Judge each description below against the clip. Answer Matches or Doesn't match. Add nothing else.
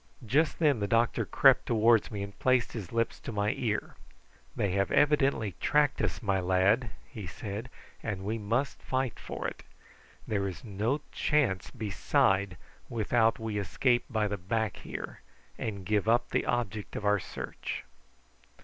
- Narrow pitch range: Doesn't match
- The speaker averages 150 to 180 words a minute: Matches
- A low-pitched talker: Matches